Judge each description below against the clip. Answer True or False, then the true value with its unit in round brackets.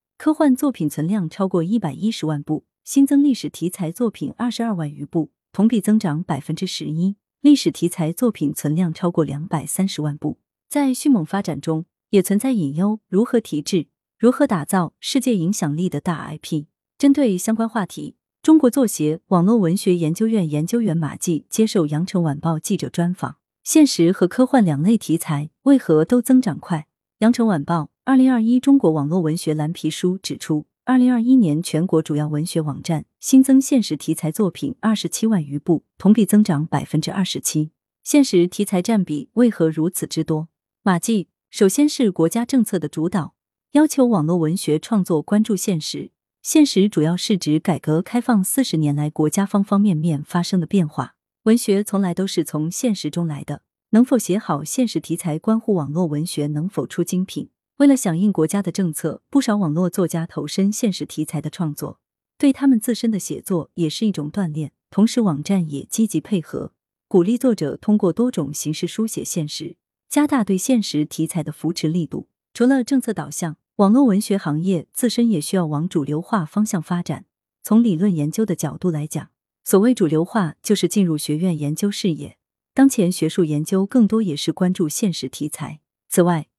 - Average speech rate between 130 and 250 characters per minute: False (290 characters per minute)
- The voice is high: False (180 Hz)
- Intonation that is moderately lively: False (5.9 semitones)